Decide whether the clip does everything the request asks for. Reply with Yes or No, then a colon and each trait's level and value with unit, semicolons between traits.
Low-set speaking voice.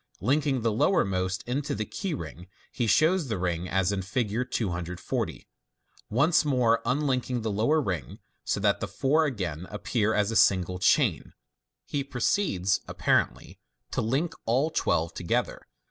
Yes: low, 115 Hz